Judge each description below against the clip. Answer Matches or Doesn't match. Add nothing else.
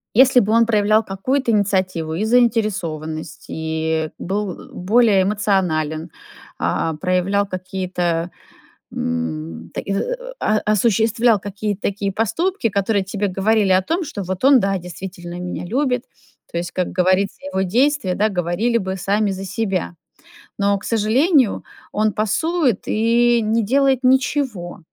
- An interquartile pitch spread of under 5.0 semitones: Matches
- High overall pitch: Matches